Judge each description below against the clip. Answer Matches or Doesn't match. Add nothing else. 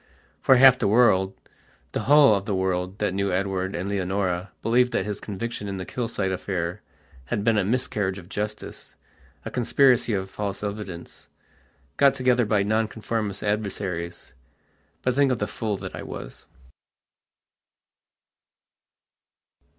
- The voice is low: Matches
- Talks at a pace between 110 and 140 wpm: Matches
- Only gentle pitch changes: Doesn't match